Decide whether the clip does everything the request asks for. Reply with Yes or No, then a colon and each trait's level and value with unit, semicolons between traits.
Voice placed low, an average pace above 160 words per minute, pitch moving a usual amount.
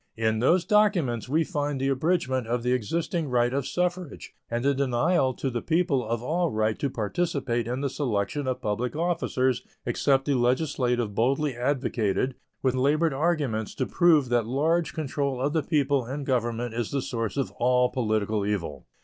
Yes: low, 130 Hz; average, 175 wpm; average, 3.8 semitones